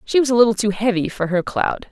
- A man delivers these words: No, female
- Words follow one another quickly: Yes, fast, 280 wpm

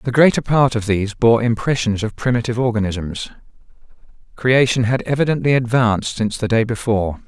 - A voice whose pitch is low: Yes, low, 115 Hz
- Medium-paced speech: Yes, average, 150 wpm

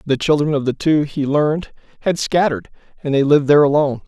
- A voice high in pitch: No, medium, 145 Hz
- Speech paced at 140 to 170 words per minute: No, fast, 205 wpm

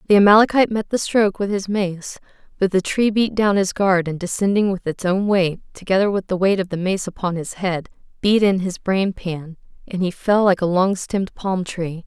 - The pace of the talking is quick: Yes, fast, 225 wpm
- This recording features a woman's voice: Yes, female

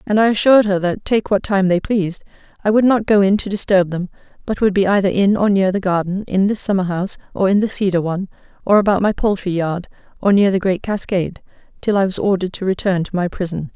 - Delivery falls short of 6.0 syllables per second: No, 6.3 syllables/s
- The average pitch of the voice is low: No, high, 195 Hz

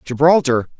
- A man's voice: Yes, male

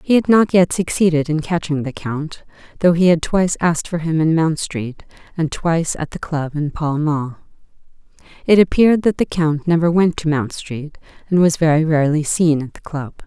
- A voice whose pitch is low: No, medium, 160 Hz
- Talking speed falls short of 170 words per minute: No, fast, 205 wpm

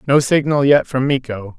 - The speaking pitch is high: No, low, 135 Hz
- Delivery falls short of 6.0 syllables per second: Yes, 4.9 syllables/s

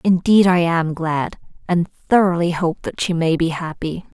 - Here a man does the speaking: No, female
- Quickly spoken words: No, average, 170 wpm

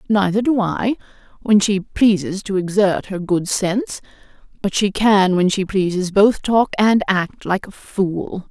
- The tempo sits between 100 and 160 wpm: Yes, average, 155 wpm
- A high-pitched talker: Yes, high, 200 Hz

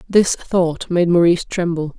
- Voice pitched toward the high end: No, medium, 175 Hz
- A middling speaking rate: Yes, average, 150 wpm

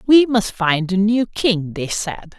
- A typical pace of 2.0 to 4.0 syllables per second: Yes, 3.6 syllables/s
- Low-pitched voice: No, high, 205 Hz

